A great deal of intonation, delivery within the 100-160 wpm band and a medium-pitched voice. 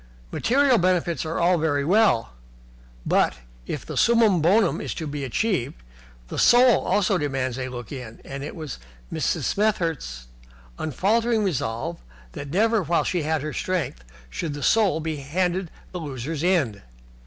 Yes: wide, 5.8 semitones; average, 155 wpm; medium, 165 Hz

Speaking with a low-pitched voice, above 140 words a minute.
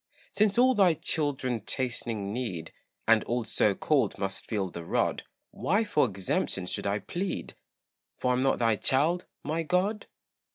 Yes: low, 130 Hz; average, 160 wpm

